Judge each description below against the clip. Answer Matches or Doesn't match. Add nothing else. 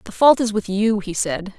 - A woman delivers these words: Matches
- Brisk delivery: Matches